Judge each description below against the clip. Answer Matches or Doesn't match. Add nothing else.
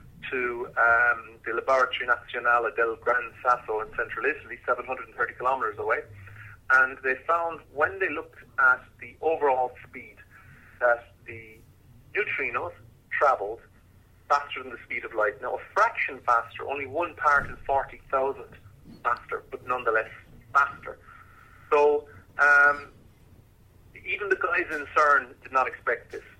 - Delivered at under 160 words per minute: Matches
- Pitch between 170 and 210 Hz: Doesn't match